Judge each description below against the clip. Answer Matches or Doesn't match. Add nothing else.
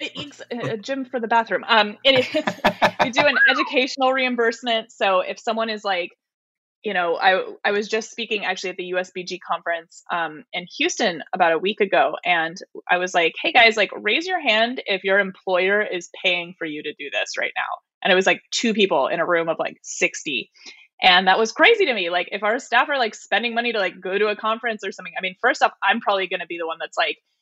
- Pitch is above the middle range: Matches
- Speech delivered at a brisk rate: Matches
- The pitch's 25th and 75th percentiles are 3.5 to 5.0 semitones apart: Matches